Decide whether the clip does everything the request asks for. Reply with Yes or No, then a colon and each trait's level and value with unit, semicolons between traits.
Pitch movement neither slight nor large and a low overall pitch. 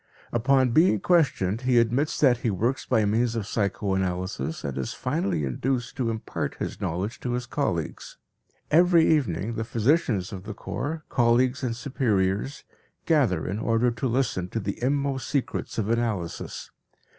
Yes: average, 4.9 semitones; low, 115 Hz